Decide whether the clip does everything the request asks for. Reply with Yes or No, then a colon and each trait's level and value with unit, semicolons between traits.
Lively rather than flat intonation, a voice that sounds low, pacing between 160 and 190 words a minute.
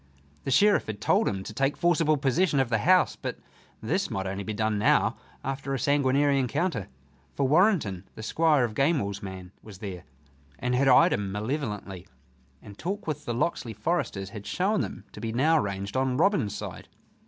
Yes: wide, 6.7 semitones; low, 125 Hz; average, 185 wpm